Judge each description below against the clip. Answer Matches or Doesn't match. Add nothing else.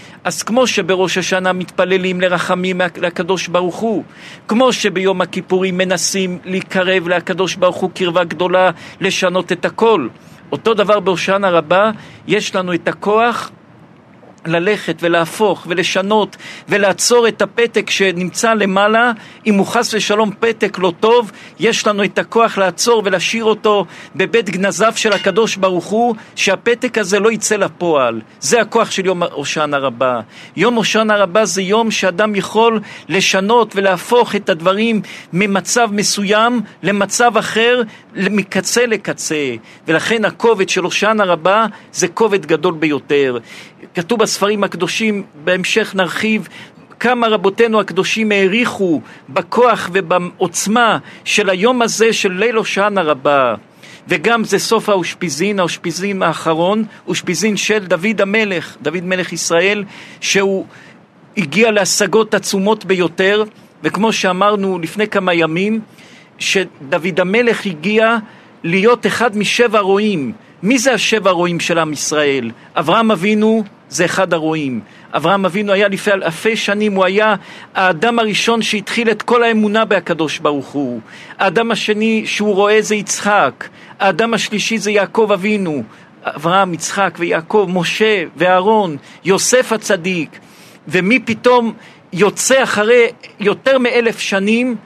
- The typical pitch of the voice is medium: Doesn't match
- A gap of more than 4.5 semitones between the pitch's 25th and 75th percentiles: Doesn't match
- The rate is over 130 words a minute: Doesn't match